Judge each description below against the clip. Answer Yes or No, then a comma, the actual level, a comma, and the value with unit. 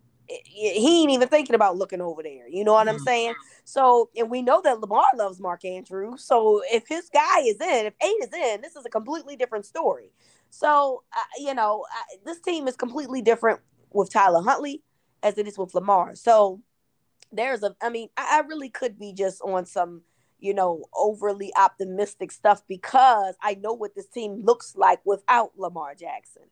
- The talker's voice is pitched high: Yes, high, 225 Hz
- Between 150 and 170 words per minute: No, average, 190 wpm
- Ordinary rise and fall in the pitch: No, wide, 5.8 semitones